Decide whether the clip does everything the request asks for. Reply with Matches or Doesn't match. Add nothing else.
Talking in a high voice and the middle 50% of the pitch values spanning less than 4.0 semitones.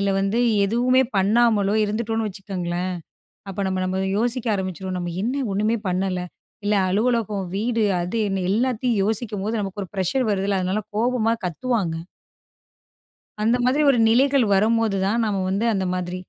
Matches